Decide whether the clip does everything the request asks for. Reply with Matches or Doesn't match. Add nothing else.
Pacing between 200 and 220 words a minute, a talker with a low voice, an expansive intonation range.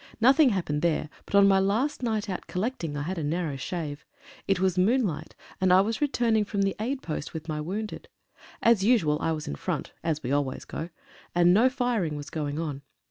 Doesn't match